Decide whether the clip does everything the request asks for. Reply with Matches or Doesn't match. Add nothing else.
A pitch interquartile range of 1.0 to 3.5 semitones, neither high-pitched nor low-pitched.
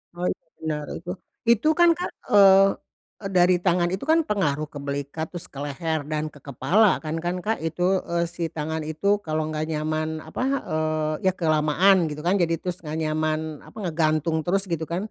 Matches